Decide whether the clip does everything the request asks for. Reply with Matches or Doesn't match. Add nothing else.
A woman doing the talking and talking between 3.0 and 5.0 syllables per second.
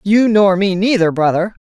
Matches